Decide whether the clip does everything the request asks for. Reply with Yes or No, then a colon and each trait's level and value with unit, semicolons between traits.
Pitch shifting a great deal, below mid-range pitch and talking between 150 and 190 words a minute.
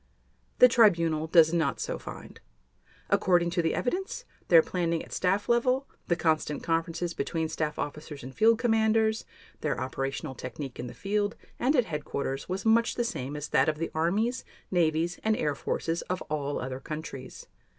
No: wide, 6.1 semitones; medium, 165 Hz; average, 170 wpm